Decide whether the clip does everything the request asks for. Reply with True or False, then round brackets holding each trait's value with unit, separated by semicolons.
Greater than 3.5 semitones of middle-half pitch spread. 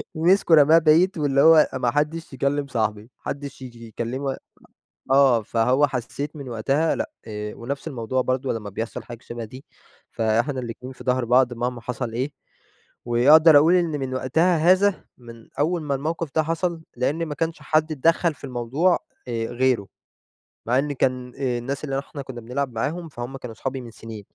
True (4.3 semitones)